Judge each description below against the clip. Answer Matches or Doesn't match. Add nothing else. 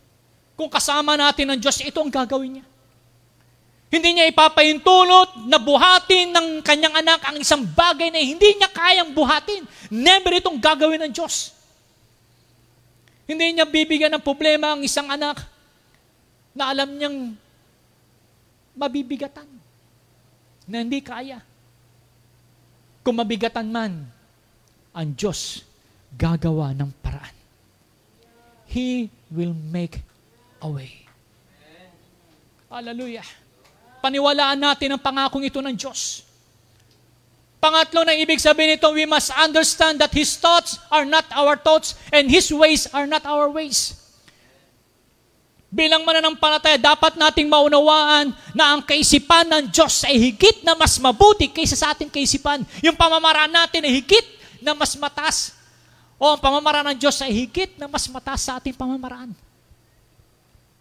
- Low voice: Doesn't match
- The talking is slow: Doesn't match